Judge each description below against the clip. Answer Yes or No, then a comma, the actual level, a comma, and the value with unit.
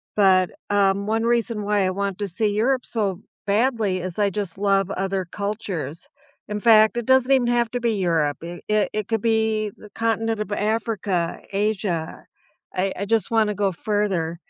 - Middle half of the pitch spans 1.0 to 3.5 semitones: Yes, narrow, 2.6 semitones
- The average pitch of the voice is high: Yes, high, 205 Hz